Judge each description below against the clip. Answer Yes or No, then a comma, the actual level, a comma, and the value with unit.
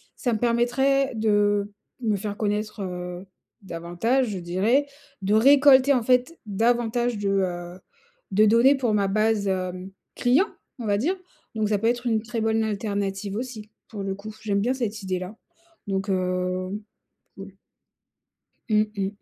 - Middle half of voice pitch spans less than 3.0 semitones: No, average, 3.6 semitones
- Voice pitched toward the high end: Yes, high, 210 Hz